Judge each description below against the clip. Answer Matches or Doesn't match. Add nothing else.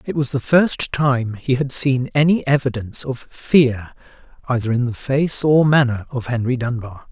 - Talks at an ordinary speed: Matches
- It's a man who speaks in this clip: Matches